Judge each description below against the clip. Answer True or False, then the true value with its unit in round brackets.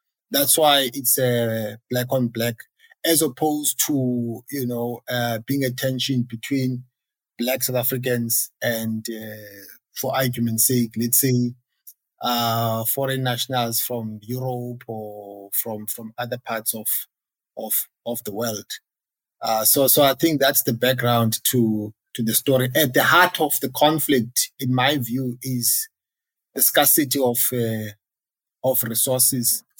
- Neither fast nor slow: True (145 wpm)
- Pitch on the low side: True (125 Hz)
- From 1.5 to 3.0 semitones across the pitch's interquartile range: True (2.7 semitones)